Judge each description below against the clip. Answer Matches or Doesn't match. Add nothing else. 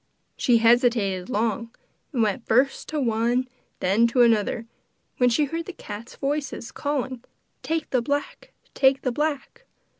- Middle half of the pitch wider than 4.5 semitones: Doesn't match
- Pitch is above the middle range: Matches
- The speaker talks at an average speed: Matches